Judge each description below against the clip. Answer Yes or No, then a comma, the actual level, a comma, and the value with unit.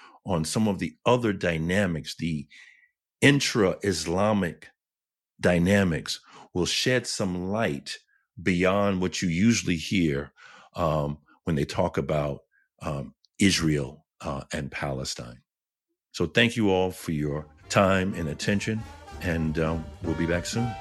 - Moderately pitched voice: No, very low, 85 Hz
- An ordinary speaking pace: No, slow, 125 wpm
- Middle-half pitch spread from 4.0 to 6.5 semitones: Yes, average, 4.5 semitones